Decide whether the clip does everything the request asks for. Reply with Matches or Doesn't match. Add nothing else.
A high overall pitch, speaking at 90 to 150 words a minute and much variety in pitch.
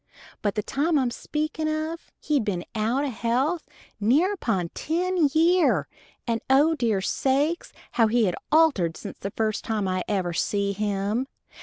Doesn't match